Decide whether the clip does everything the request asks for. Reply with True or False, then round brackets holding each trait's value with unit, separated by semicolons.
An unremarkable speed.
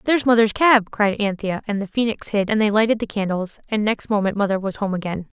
False (235 wpm)